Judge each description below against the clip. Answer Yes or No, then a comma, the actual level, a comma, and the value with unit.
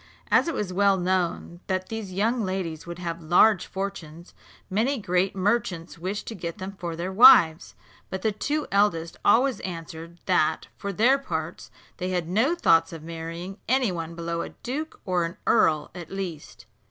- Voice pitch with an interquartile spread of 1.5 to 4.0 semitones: Yes, average, 3.7 semitones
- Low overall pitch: No, medium, 185 Hz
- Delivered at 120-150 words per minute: No, average, 170 wpm